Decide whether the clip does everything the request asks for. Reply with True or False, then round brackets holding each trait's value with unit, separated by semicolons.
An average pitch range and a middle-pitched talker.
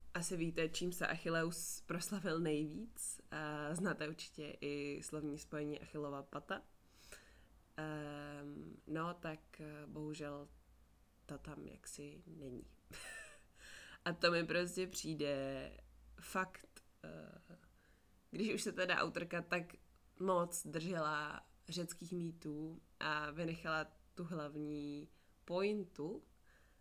True (3.0 semitones; 155 Hz)